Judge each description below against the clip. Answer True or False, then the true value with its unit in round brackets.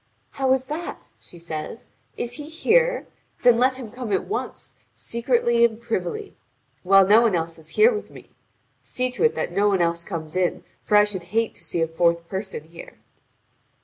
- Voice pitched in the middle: False (220 Hz)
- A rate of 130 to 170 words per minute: False (185 wpm)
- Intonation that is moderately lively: False (6.7 semitones)